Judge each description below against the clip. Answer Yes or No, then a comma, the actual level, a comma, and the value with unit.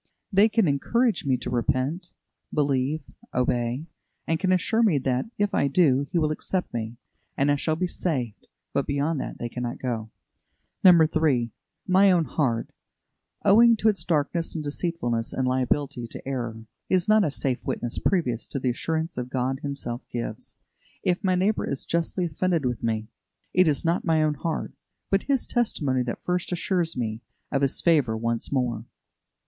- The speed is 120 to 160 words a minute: No, average, 170 wpm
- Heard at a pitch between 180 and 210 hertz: No, medium, 145 Hz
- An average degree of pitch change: No, wide, 6.0 semitones